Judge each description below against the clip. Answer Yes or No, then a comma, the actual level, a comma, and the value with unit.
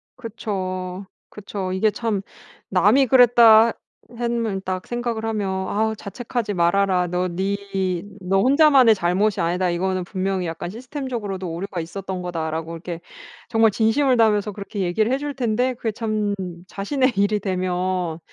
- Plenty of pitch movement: No, average, 3.7 semitones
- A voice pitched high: Yes, high, 200 Hz